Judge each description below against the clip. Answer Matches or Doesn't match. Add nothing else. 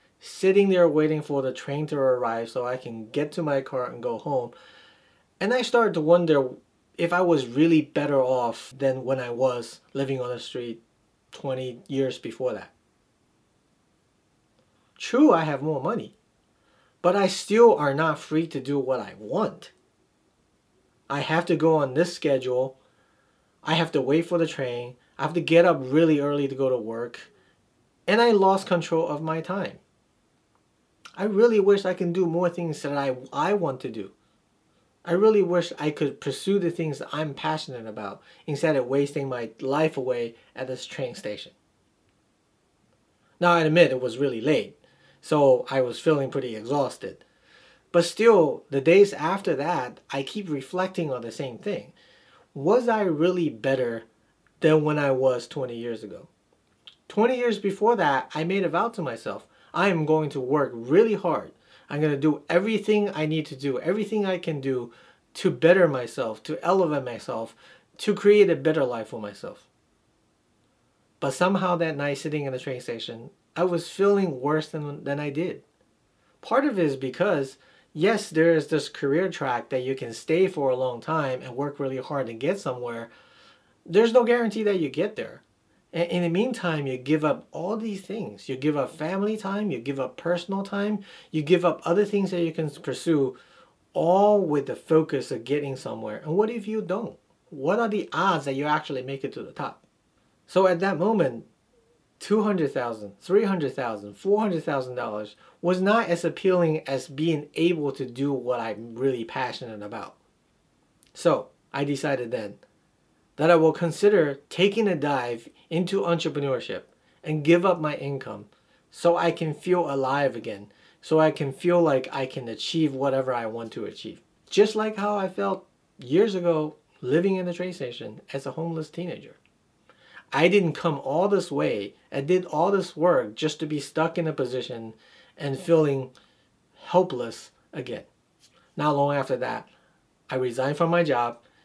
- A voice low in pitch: Doesn't match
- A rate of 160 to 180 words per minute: Matches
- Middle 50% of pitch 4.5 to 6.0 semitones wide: Matches